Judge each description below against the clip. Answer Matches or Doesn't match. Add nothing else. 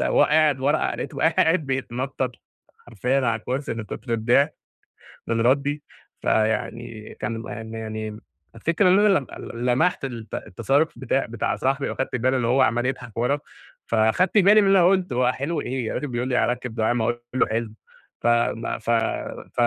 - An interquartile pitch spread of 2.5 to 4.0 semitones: Matches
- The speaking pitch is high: Doesn't match